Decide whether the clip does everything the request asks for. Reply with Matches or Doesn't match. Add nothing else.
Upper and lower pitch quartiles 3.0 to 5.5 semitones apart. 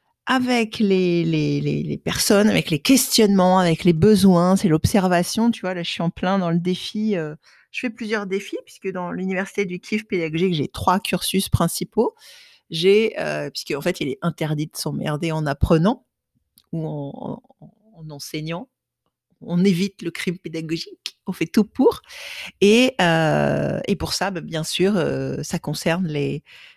Matches